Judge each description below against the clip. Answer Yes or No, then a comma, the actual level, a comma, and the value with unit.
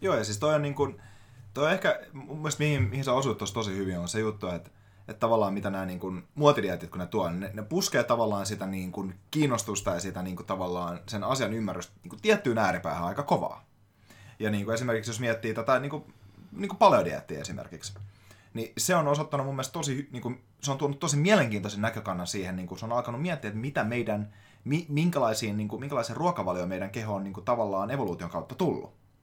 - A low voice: Yes, low, 110 Hz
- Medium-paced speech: No, fast, 200 wpm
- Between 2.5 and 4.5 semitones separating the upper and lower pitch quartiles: No, wide, 5.6 semitones